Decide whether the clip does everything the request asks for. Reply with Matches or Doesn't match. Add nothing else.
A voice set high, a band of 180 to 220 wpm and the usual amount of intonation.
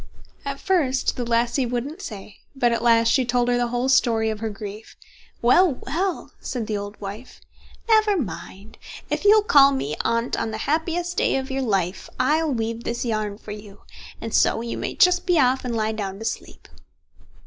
Matches